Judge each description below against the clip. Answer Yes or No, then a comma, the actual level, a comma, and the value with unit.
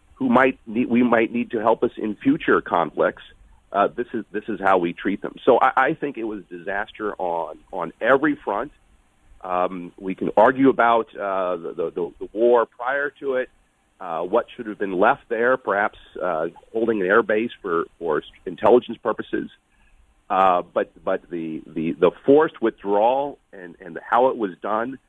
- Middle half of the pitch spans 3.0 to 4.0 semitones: No, average, 4.8 semitones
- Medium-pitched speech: No, low, 120 Hz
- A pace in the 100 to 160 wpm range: No, average, 180 wpm